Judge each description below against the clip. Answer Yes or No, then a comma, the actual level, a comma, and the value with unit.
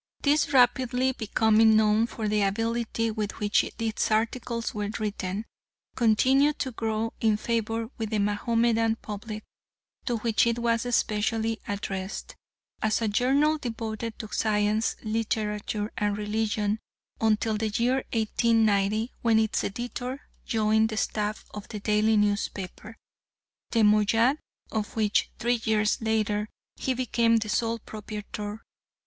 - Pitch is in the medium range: No, high, 220 Hz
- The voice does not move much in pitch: Yes, narrow, 1.6 semitones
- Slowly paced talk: Yes, slow, 130 wpm